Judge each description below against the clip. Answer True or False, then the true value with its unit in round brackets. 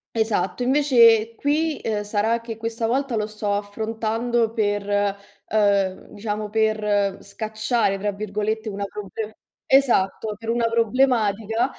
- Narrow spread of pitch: True (1.9 semitones)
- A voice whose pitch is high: True (220 Hz)